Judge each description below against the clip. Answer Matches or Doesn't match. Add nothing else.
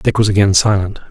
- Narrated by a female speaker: Doesn't match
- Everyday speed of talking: Doesn't match